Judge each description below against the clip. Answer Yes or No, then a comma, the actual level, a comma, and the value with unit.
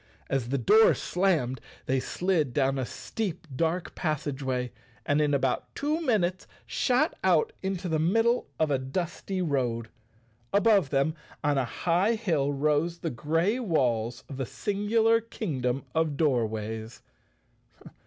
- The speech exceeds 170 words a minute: No, slow, 135 wpm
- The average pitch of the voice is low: No, medium, 155 Hz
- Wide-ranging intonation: Yes, wide, 6.3 semitones